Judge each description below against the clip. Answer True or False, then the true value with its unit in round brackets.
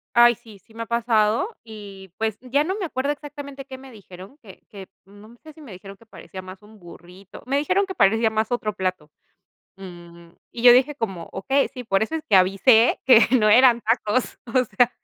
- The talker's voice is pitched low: False (225 Hz)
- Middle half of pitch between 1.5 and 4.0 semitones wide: False (5.0 semitones)